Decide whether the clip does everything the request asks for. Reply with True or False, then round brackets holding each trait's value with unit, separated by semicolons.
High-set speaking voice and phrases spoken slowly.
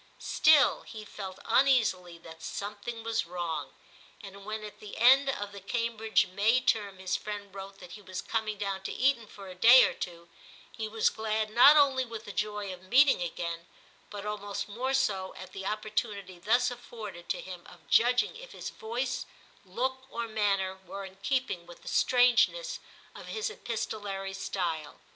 False (210 Hz; 175 wpm)